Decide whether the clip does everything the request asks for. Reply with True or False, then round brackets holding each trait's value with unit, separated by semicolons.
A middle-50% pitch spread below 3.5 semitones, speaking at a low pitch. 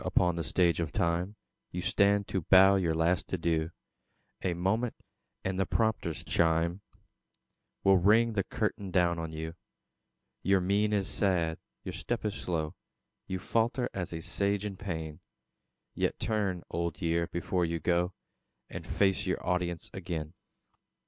True (2.8 semitones; 90 Hz)